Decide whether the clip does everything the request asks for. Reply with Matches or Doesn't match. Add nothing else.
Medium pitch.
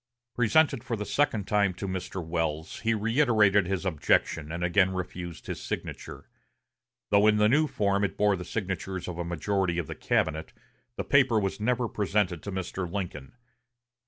Doesn't match